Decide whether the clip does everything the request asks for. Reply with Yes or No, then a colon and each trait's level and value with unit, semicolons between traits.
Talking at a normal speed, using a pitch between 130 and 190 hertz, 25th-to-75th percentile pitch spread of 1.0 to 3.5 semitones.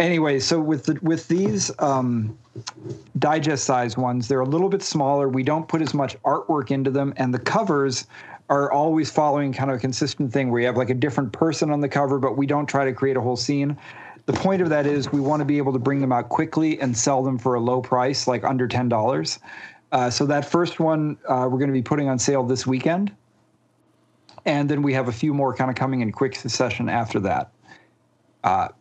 No: fast, 225 wpm; medium, 140 Hz; average, 2.8 semitones